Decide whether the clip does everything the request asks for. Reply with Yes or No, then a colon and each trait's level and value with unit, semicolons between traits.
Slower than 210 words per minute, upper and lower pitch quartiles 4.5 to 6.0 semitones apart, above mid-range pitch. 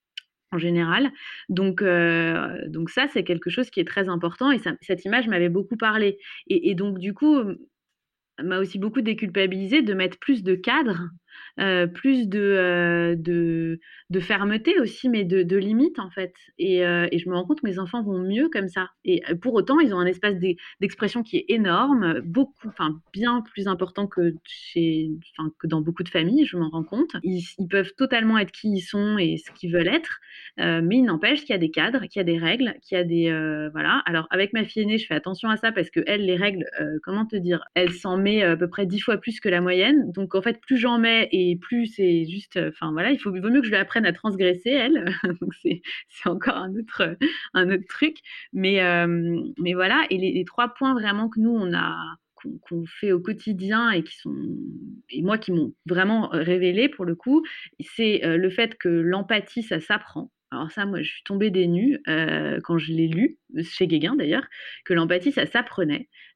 No: fast, 220 wpm; average, 5.0 semitones; high, 195 Hz